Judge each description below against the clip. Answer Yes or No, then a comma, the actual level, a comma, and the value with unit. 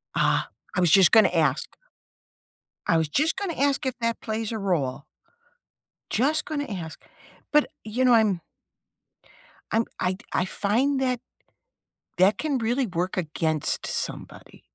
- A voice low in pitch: No, high, 220 Hz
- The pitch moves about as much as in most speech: No, wide, 6.4 semitones